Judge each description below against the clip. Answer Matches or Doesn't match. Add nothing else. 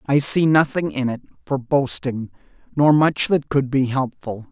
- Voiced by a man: Matches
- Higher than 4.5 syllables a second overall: Doesn't match